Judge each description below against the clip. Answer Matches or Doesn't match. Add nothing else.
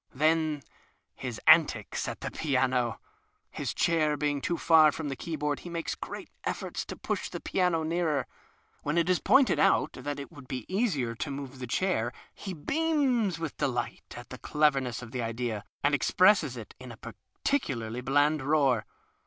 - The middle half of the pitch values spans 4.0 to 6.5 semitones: Matches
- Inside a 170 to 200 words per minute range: Matches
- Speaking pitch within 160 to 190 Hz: Doesn't match